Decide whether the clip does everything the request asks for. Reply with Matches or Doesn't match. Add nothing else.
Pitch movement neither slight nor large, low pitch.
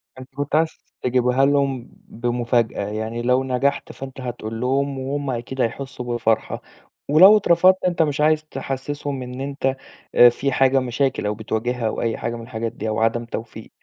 Matches